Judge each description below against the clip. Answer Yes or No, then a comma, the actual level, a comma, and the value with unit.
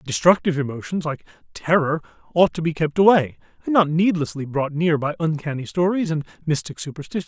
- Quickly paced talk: No, average, 165 wpm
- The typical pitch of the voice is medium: Yes, medium, 160 Hz